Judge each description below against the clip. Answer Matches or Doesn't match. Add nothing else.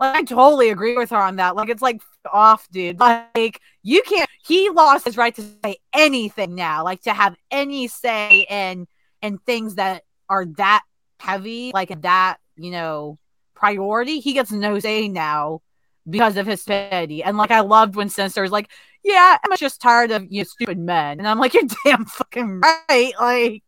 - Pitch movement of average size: Matches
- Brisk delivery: Doesn't match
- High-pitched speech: Matches